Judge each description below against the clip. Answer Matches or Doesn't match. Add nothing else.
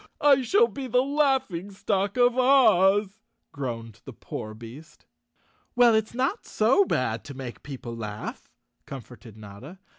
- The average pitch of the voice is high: Matches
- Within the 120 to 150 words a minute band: Matches